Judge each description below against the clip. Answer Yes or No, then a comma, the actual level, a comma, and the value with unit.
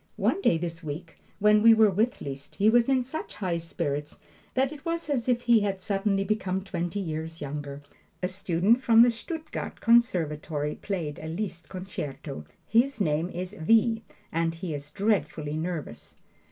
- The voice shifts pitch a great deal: Yes, wide, 5.9 semitones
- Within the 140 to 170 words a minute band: Yes, average, 165 wpm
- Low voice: No, medium, 185 Hz